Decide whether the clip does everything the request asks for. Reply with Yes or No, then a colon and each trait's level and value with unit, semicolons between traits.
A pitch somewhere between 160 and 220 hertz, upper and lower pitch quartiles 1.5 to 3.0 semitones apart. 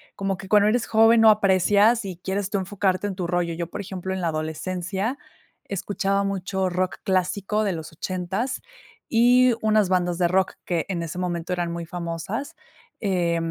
Yes: high, 190 Hz; narrow, 2.6 semitones